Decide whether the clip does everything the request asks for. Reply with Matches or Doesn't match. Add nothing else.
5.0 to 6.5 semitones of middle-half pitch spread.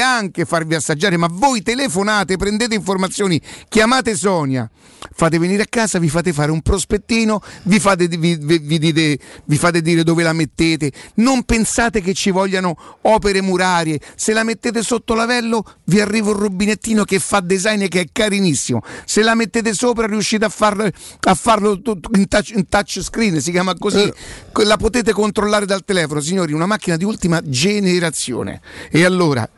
Doesn't match